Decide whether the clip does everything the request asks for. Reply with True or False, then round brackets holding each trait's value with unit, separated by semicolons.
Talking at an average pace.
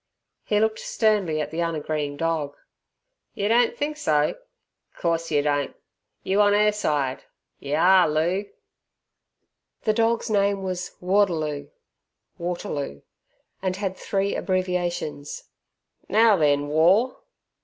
False (115 wpm)